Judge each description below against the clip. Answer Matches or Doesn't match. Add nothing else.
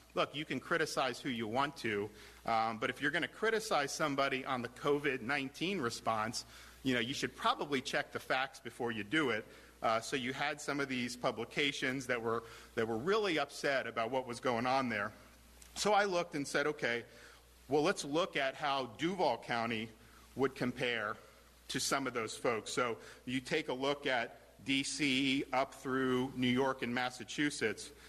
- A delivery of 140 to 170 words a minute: Doesn't match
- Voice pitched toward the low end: Matches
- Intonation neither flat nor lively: Matches